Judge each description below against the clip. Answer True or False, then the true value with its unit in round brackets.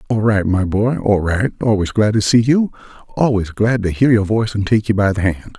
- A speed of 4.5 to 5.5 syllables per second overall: True (5.3 syllables/s)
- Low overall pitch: True (105 Hz)